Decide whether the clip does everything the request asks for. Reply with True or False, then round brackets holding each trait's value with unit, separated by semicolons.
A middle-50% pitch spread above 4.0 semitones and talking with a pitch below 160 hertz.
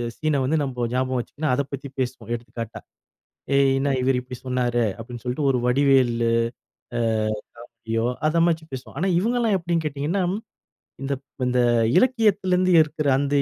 True (4.4 semitones; 140 Hz)